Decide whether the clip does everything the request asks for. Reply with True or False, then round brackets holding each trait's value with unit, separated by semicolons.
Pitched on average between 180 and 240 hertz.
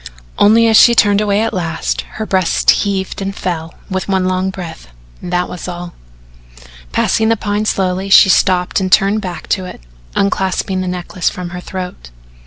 True (190 Hz)